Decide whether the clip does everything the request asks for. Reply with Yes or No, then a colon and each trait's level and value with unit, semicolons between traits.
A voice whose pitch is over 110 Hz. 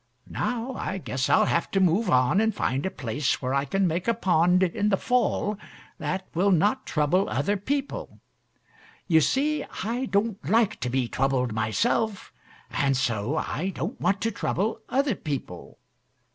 Yes: medium, 185 Hz